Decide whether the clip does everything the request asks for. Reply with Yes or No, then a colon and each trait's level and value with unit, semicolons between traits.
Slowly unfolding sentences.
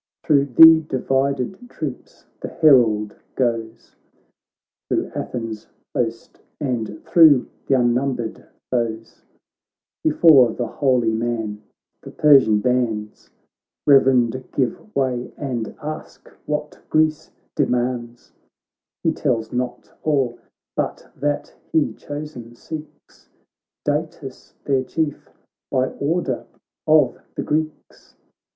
Yes: slow, 100 wpm